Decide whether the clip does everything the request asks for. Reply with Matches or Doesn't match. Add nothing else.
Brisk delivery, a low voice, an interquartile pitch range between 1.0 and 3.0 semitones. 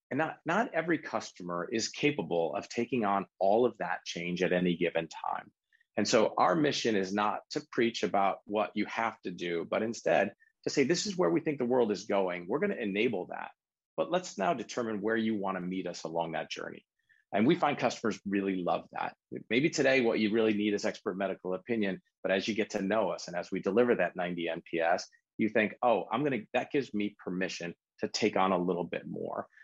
Doesn't match